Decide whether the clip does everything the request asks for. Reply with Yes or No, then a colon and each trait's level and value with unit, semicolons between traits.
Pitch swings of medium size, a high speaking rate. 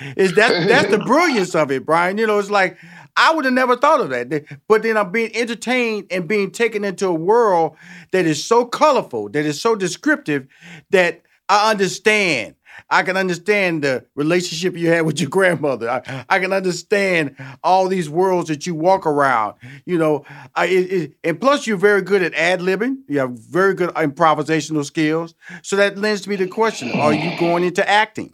No: average, 4.6 semitones; average, 195 wpm